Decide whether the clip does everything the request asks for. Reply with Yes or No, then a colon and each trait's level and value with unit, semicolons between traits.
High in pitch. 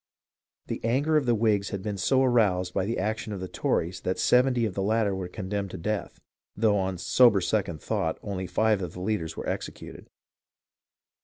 No: low, 100 Hz